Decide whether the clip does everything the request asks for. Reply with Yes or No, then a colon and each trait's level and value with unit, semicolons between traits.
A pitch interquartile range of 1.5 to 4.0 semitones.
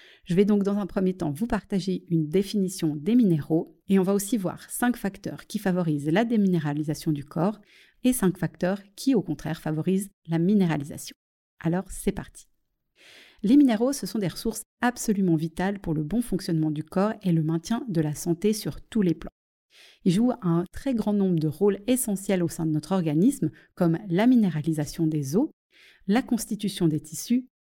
No: average, 4.6 semitones